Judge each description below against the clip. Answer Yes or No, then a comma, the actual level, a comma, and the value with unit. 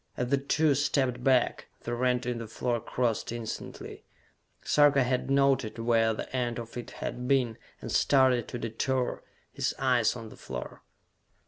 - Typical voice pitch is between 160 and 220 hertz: No, low, 125 Hz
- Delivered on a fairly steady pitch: Yes, narrow, 2.2 semitones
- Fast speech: No, average, 160 wpm